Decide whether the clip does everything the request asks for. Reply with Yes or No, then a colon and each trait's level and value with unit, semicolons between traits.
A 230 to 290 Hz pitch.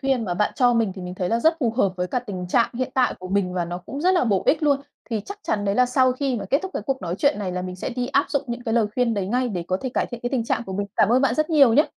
Yes: high, 235 Hz